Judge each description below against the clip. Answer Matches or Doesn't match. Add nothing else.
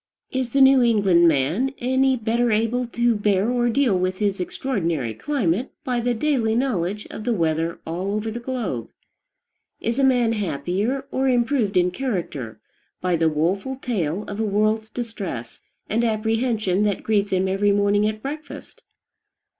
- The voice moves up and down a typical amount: Matches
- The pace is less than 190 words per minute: Matches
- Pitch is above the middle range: Matches